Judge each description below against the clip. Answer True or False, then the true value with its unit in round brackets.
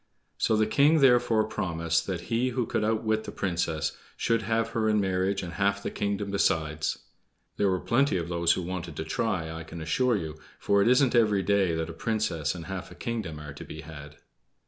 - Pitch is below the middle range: True (95 Hz)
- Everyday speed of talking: False (210 wpm)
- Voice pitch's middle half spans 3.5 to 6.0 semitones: True (5.1 semitones)